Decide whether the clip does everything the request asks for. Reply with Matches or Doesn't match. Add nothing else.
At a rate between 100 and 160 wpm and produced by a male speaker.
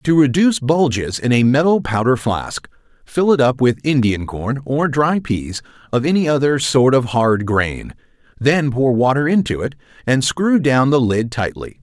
Doesn't match